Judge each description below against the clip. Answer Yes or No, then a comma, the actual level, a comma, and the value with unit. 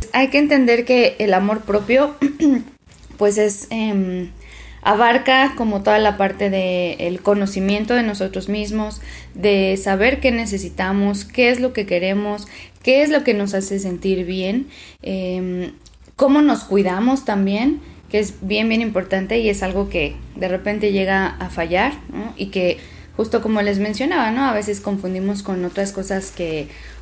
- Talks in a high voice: Yes, high, 205 Hz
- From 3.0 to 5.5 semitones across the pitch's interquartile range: Yes, average, 3.7 semitones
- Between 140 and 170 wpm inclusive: Yes, average, 155 wpm